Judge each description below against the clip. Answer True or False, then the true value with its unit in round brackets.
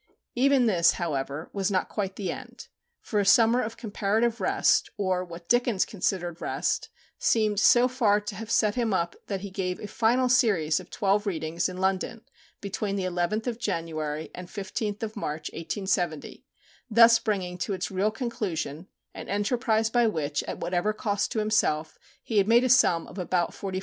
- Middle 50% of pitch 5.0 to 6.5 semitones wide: False (3.9 semitones)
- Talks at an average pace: True (180 wpm)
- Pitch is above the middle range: True (200 Hz)